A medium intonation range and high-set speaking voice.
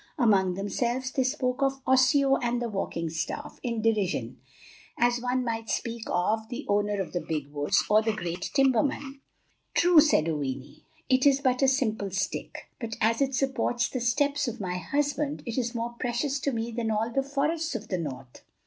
Yes: average, 4.7 semitones; high, 235 Hz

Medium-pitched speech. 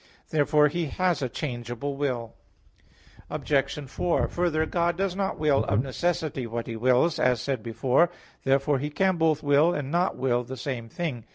Yes: medium, 145 Hz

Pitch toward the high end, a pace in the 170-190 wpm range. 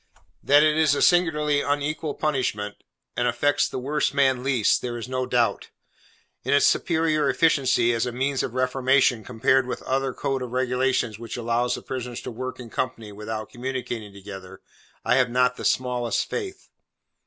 No: low, 130 Hz; average, 175 wpm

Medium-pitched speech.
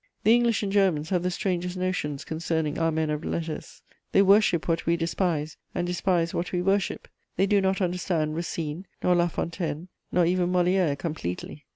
Yes: medium, 175 Hz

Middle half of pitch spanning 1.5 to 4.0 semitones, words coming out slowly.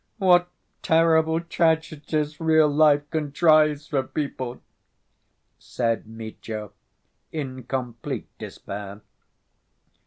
No: average, 4.4 semitones; slow, 80 wpm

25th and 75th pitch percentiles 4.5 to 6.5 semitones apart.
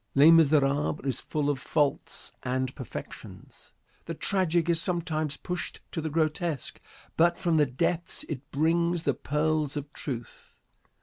No: average, 2.9 semitones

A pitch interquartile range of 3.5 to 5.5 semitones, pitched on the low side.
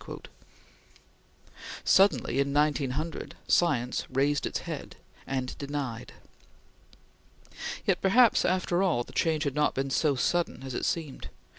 No: average, 4.0 semitones; medium, 145 Hz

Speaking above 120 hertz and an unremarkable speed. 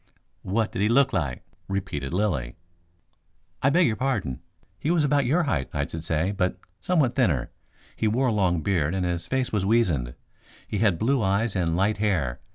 No: low, 100 Hz; average, 185 wpm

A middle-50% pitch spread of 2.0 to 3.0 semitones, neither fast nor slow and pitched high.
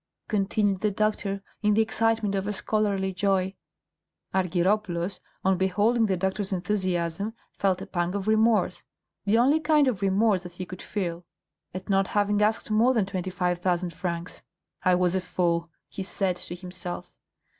Yes: narrow, 2.6 semitones; average, 165 wpm; high, 195 Hz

